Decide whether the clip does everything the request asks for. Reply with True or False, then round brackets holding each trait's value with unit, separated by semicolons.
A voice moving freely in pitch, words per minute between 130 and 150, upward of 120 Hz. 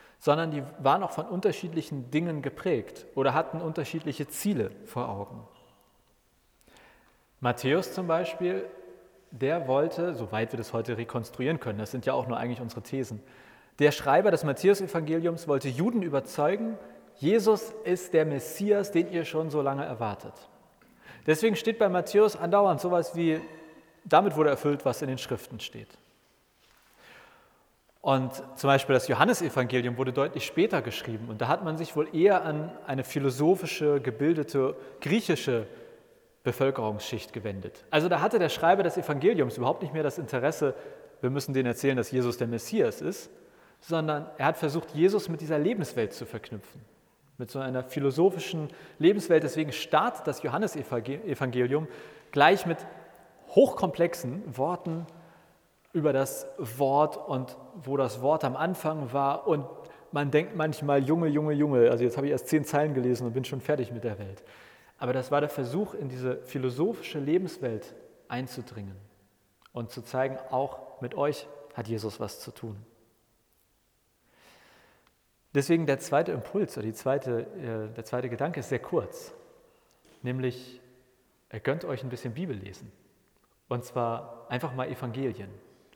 False (4.5 semitones; 145 wpm; 140 Hz)